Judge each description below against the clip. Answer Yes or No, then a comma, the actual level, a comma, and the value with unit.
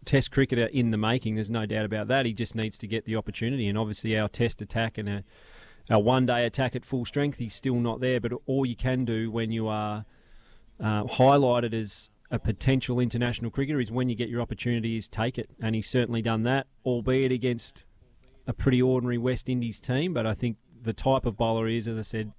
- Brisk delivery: Yes, fast, 220 wpm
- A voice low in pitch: Yes, low, 115 Hz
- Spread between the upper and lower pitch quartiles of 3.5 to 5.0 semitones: No, narrow, 2.4 semitones